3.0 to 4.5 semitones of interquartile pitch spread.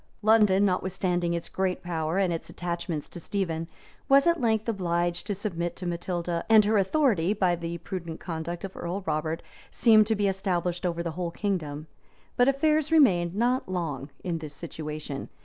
Yes: average, 3.3 semitones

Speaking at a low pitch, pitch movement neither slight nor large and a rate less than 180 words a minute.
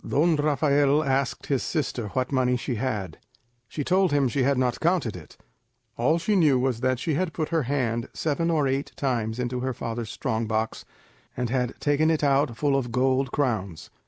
No: low, 130 Hz; average, 3.4 semitones; average, 190 wpm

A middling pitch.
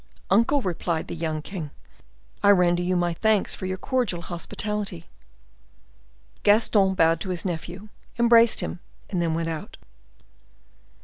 Yes: medium, 180 Hz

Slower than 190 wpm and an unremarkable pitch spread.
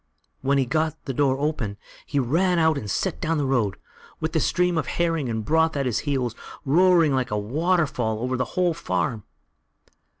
No: average, 195 wpm; average, 4.6 semitones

